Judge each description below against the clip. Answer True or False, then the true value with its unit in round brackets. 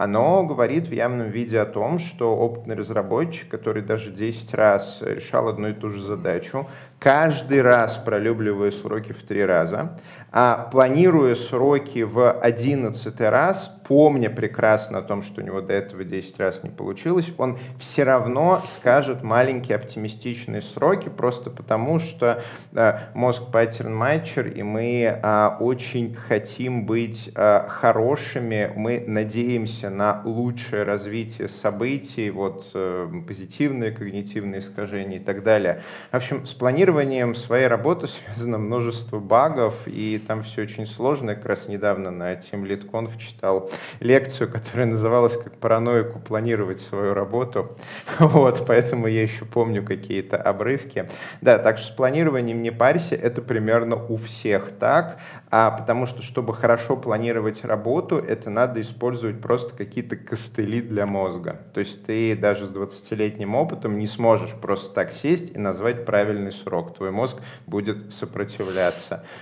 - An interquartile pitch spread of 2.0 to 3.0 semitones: True (2.7 semitones)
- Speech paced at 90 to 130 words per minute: False (140 wpm)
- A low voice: True (115 Hz)